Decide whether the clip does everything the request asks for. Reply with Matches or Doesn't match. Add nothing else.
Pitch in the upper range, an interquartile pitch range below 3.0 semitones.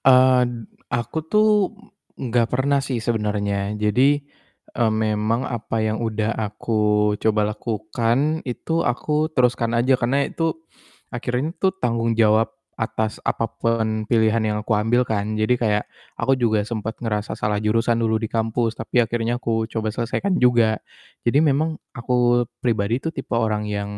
Doesn't match